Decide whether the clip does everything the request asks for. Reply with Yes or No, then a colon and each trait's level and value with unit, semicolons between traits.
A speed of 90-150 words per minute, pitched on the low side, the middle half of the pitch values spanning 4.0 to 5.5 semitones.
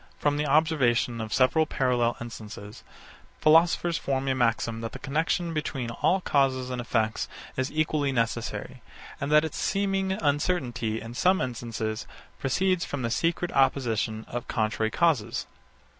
Yes: average, 145 wpm; low, 130 Hz; average, 5.2 semitones